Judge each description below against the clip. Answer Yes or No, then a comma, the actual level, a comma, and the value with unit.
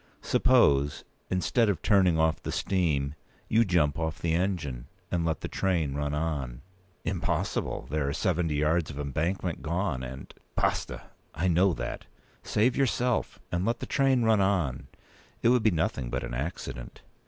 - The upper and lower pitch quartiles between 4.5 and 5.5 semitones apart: Yes, average, 5.1 semitones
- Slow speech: No, average, 160 wpm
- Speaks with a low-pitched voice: Yes, very low, 85 Hz